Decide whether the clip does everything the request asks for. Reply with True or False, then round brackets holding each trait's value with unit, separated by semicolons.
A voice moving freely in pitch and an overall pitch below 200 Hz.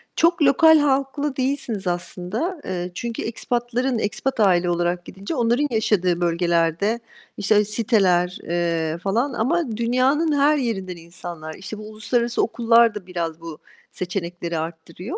False (6.2 semitones; 210 Hz)